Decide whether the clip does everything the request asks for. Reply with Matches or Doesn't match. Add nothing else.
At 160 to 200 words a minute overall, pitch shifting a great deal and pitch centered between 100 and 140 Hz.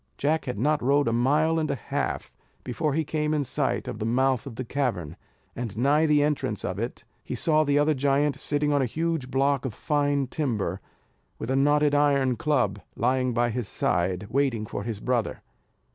Doesn't match